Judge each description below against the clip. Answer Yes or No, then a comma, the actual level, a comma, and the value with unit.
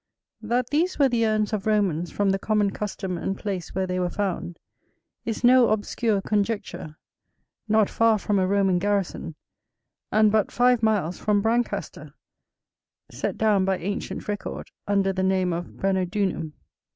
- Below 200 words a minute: Yes, average, 150 wpm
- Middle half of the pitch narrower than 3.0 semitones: Yes, narrow, 2.5 semitones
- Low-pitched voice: No, high, 205 Hz